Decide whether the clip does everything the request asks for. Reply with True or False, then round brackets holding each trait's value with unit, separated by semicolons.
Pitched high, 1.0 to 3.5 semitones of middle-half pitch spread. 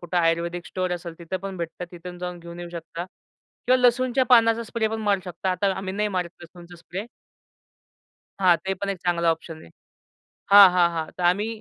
False (180 Hz; 2.7 semitones)